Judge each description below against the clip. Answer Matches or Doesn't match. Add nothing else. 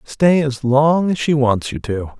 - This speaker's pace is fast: Matches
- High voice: Doesn't match